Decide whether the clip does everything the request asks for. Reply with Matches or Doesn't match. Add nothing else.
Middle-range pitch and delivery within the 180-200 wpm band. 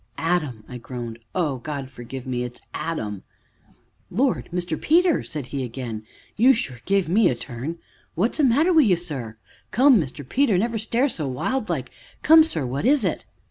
Matches